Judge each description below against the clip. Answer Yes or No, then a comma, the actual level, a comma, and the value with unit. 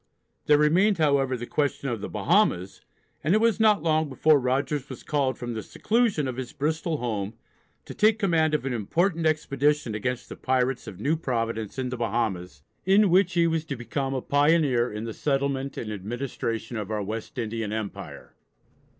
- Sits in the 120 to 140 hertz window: Yes, low, 135 Hz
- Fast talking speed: No, average, 185 wpm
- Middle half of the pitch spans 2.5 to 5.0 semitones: No, wide, 5.4 semitones